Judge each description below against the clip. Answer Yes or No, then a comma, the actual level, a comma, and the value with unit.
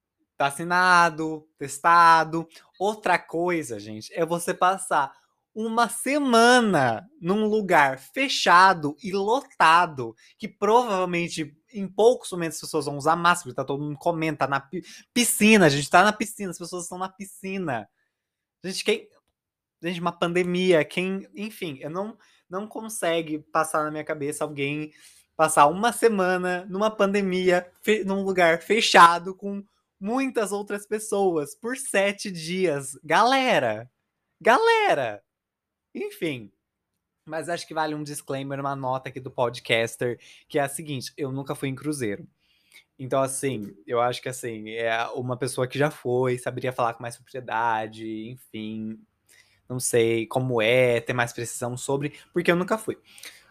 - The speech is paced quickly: No, average, 140 wpm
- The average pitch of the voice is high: No, medium, 165 Hz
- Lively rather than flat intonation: Yes, wide, 6.3 semitones